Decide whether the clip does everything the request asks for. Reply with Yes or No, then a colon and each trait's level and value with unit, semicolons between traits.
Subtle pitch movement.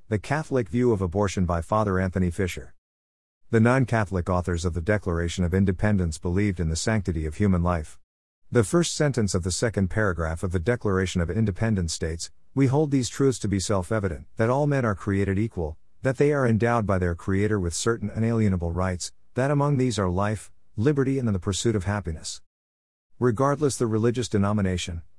No: average, 4.5 semitones